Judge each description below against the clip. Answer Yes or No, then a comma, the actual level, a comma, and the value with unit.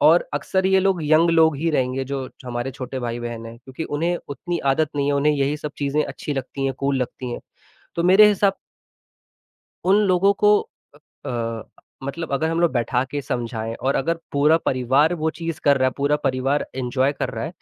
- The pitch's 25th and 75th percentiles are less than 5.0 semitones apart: Yes, average, 4.2 semitones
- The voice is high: No, medium, 140 Hz